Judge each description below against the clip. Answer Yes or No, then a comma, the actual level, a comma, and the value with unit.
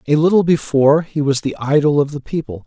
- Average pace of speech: No, fast, 225 wpm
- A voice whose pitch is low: No, medium, 145 Hz